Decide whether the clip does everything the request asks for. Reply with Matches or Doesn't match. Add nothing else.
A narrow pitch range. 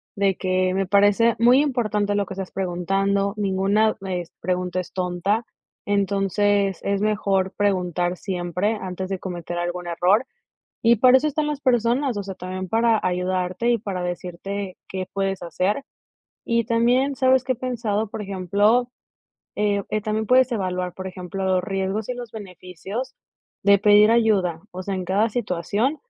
Doesn't match